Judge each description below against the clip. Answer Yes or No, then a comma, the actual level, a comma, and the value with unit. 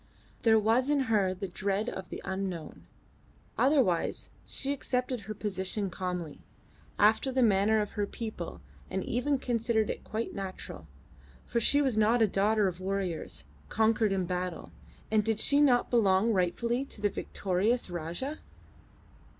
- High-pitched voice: Yes, high, 210 Hz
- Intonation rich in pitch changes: No, average, 3.9 semitones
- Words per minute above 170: No, average, 150 wpm